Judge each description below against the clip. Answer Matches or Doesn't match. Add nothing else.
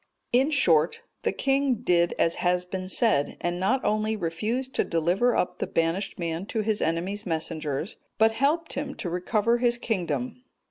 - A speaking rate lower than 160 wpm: Doesn't match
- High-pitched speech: Matches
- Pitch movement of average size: Doesn't match